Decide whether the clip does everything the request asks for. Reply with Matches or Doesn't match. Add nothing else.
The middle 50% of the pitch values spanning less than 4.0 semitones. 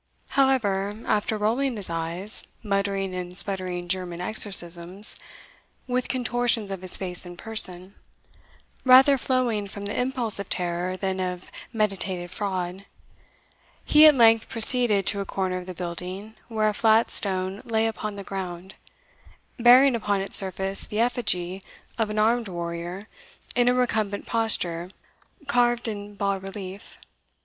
Matches